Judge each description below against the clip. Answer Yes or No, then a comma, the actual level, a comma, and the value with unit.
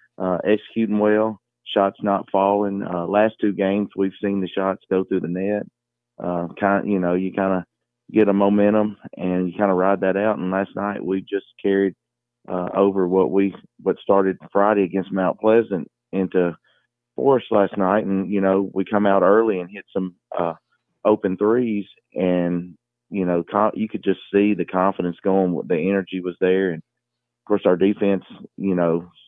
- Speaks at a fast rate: No, average, 185 wpm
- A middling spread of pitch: No, narrow, 2.0 semitones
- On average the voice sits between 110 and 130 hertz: No, very low, 95 Hz